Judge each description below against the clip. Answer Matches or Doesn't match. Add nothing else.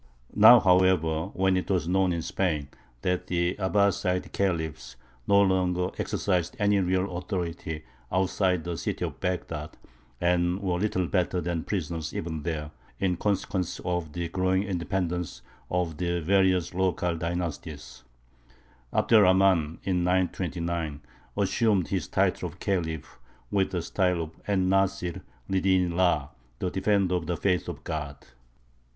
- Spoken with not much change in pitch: Matches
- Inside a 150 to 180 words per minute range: Doesn't match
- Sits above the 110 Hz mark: Doesn't match